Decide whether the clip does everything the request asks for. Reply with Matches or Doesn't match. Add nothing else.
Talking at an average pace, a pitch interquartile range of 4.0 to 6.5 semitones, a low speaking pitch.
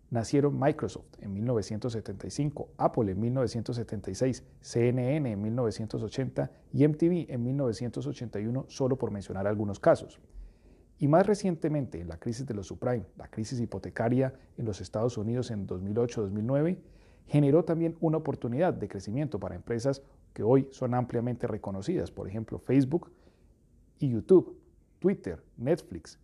Doesn't match